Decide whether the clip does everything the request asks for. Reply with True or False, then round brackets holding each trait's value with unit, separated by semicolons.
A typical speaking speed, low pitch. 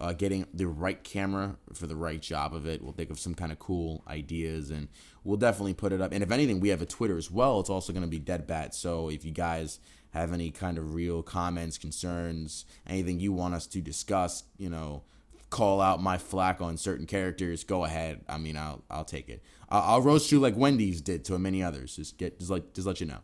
False (240 wpm; 85 Hz)